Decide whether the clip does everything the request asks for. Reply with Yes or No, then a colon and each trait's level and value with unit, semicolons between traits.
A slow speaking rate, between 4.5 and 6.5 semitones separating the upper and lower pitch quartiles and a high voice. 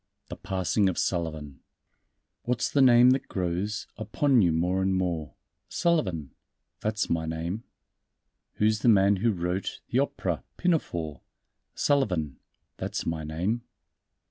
No: slow, 130 wpm; wide, 5.4 semitones; very low, 95 Hz